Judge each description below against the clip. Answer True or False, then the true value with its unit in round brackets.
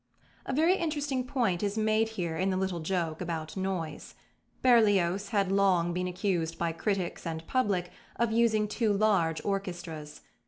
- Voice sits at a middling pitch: False (195 Hz)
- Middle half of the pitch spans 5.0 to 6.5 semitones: False (4.1 semitones)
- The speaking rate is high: False (155 wpm)